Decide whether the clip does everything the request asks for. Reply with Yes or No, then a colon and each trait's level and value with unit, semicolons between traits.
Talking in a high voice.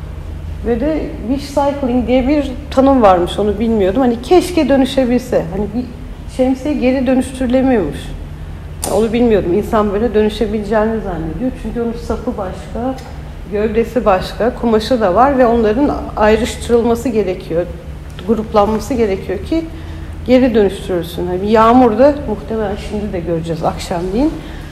Yes: high, 225 Hz